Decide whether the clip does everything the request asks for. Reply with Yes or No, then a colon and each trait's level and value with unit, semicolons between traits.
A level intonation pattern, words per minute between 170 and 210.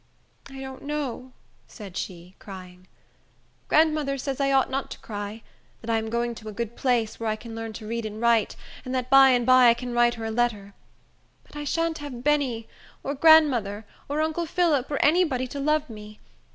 No: average, 4.2 semitones; fast, 205 wpm